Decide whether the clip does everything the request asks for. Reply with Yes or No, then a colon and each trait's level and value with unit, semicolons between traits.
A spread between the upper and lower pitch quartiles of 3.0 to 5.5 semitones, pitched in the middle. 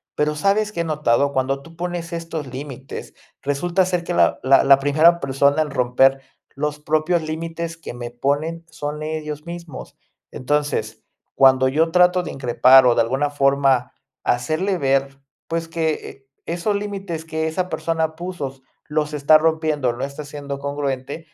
Yes: average, 3.3 semitones; medium, 150 Hz